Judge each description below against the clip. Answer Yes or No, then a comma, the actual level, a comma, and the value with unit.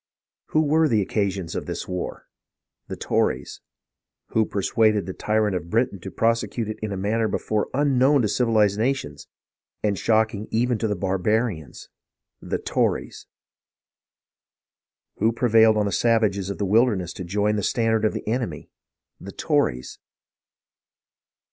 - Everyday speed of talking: Yes, average, 145 wpm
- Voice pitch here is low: Yes, low, 110 Hz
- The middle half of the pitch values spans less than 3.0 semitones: Yes, narrow, 2.6 semitones